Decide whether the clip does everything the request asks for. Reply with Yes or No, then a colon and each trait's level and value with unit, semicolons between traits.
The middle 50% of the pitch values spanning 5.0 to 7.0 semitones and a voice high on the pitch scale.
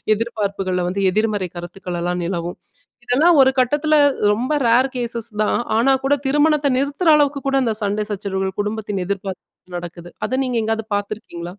Yes: average, 5.3 semitones; high, 215 Hz